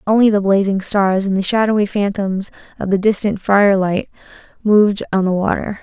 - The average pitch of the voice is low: No, high, 200 Hz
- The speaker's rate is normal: Yes, average, 165 wpm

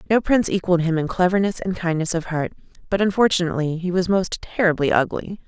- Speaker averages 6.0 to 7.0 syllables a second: Yes, 6.4 syllables/s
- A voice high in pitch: No, medium, 180 Hz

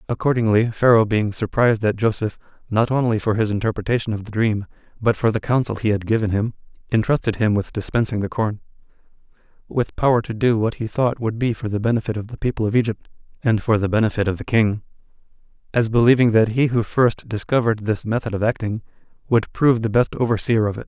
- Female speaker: No, male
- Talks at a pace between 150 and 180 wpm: No, average, 200 wpm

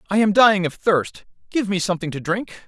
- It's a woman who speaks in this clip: No, male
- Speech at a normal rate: No, fast, 225 wpm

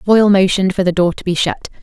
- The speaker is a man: No, female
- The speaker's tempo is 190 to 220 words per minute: No, fast, 265 wpm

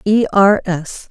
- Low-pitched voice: No, high, 195 Hz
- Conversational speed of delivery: Yes, average, 165 wpm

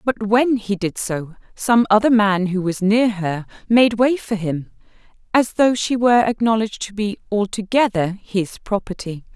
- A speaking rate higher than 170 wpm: No, average, 165 wpm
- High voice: Yes, high, 210 Hz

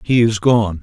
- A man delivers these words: Yes, male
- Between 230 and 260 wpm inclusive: No, fast, 215 wpm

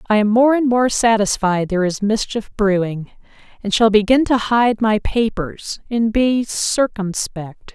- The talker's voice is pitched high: Yes, high, 220 Hz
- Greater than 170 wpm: No, average, 155 wpm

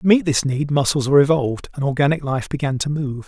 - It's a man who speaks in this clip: Yes, male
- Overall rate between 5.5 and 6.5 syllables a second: Yes, 6.3 syllables/s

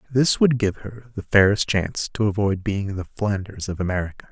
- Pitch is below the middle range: Yes, low, 105 Hz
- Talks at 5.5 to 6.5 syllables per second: No, 5.2 syllables/s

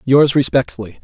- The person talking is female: No, male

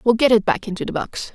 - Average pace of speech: No, fast, 315 wpm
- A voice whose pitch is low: No, high, 230 Hz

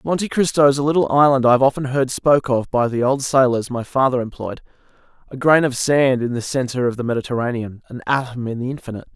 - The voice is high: No, low, 130 Hz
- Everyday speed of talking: No, fast, 215 wpm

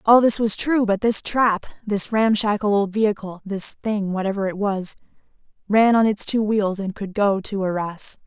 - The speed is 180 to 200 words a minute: Yes, average, 190 wpm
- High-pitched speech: Yes, high, 205 Hz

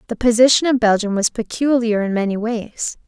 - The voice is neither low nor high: No, high, 225 Hz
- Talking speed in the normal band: Yes, average, 175 wpm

